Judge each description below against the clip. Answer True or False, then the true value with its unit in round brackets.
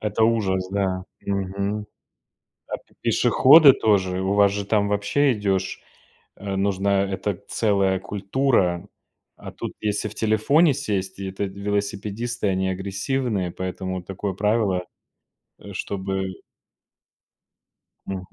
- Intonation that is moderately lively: False (1.9 semitones)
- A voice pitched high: False (100 Hz)